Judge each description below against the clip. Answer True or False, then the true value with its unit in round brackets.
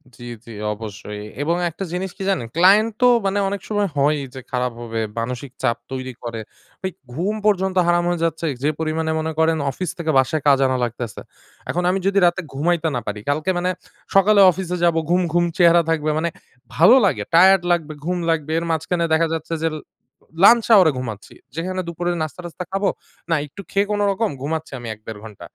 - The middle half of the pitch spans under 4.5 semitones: False (5.2 semitones)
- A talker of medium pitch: True (165 Hz)